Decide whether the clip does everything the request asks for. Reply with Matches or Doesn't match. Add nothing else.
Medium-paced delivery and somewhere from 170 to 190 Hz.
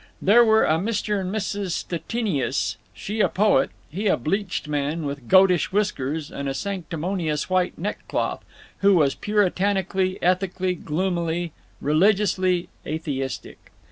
Doesn't match